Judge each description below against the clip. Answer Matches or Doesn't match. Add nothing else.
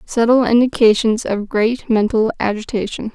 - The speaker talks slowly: Matches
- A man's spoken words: Doesn't match